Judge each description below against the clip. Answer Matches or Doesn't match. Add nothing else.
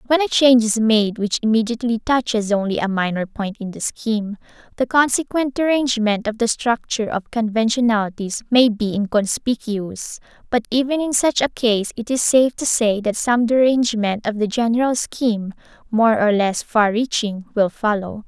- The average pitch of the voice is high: Matches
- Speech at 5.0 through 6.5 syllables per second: Matches